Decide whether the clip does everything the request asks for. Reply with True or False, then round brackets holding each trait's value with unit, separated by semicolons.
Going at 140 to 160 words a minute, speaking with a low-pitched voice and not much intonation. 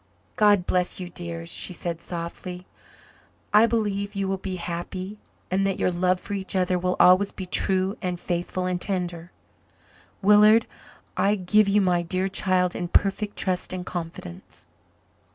False (155 wpm; 185 Hz; 1.9 semitones)